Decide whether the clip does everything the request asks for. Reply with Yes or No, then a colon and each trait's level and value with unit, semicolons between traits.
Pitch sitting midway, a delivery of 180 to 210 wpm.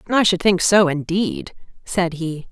No: medium, 180 Hz; average, 165 wpm